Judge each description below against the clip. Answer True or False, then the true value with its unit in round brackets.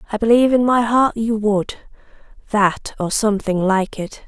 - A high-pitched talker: True (215 Hz)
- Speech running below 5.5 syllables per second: True (4.8 syllables/s)